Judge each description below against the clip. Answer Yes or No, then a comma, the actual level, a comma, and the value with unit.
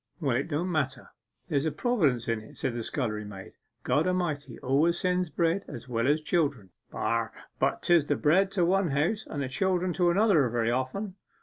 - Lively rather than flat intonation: Yes, wide, 5.8 semitones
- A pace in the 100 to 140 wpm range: No, average, 190 wpm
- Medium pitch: Yes, medium, 150 Hz